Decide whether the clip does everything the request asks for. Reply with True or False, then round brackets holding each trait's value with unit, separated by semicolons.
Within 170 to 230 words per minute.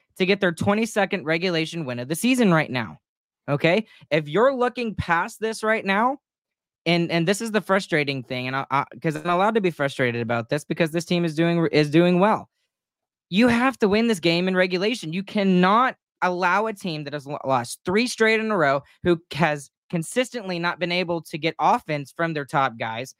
True (205 wpm)